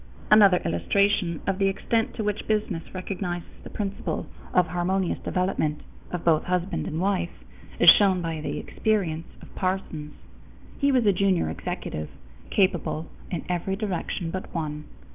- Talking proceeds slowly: No, average, 145 wpm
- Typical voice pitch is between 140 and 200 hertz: Yes, medium, 185 Hz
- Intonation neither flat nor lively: Yes, average, 3.1 semitones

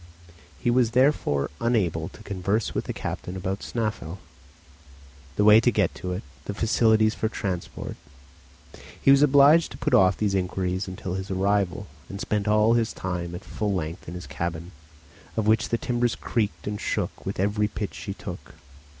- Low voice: Yes, low, 105 Hz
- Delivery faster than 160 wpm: Yes, average, 175 wpm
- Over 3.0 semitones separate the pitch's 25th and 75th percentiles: Yes, average, 3.4 semitones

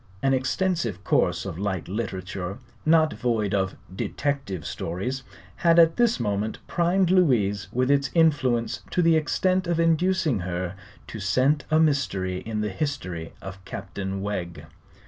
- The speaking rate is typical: Yes, average, 145 wpm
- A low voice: Yes, low, 120 Hz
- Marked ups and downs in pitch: Yes, wide, 8.7 semitones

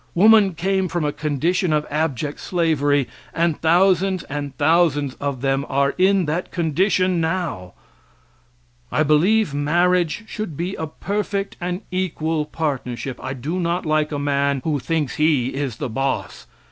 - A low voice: No, medium, 160 Hz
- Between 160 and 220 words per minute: No, average, 145 wpm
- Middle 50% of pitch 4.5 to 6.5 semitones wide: No, average, 4.0 semitones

